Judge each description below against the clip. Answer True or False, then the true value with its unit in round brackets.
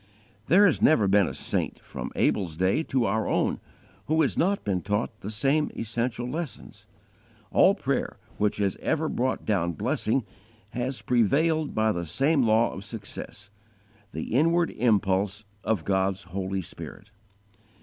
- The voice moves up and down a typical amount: False (5.8 semitones)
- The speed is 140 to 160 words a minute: True (150 wpm)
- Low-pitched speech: True (110 Hz)